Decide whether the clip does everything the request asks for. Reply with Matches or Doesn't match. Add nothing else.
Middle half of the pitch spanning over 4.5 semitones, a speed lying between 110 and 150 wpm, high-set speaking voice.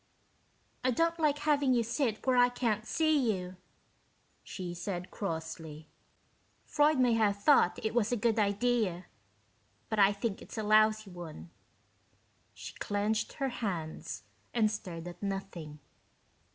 Matches